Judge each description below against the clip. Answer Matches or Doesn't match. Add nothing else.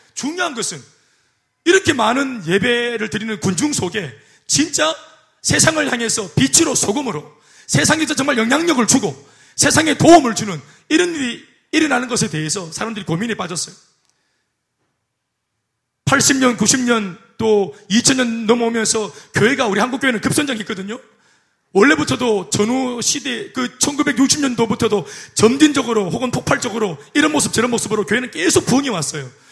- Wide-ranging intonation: Doesn't match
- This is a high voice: Matches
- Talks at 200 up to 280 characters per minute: Doesn't match